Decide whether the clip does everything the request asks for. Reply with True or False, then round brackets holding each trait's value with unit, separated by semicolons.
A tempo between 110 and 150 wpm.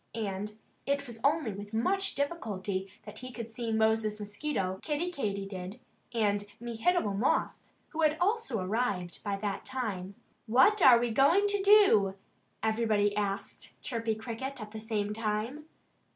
True (145 wpm)